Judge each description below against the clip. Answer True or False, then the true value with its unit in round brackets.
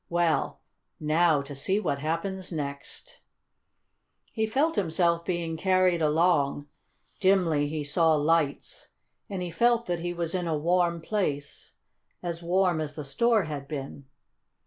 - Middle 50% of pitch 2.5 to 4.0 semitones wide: True (3.4 semitones)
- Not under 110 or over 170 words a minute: True (140 wpm)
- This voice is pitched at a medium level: True (170 Hz)